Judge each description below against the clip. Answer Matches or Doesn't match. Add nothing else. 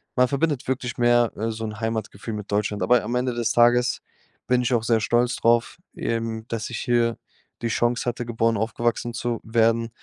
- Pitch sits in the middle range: Doesn't match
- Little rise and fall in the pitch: Matches